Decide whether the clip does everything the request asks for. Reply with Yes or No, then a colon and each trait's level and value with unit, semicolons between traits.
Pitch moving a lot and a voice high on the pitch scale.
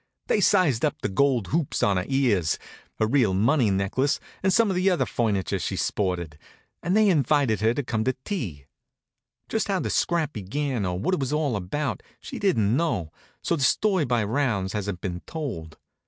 No: wide, 8.0 semitones; low, 125 Hz